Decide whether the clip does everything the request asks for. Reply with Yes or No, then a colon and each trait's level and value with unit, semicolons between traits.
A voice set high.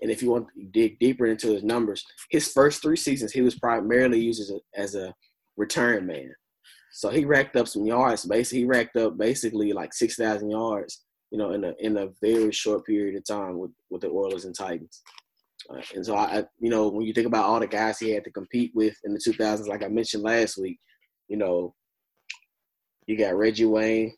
No: low, 110 Hz